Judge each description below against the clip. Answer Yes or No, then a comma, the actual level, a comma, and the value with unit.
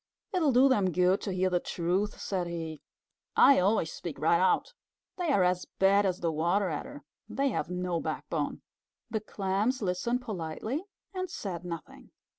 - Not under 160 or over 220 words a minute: Yes, average, 165 wpm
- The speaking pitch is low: No, medium, 185 Hz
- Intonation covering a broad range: No, average, 4.0 semitones